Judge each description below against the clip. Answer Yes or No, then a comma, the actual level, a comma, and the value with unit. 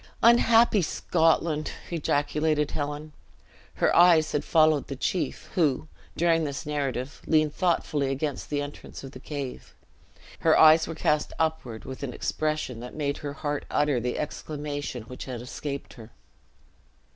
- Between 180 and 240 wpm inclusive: No, average, 145 wpm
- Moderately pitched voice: Yes, medium, 150 Hz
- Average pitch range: No, narrow, 2.3 semitones